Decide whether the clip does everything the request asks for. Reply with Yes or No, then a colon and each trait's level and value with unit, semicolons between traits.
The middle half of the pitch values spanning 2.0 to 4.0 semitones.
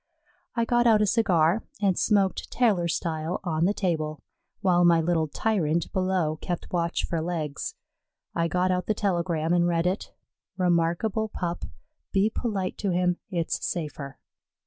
Yes: average, 2.9 semitones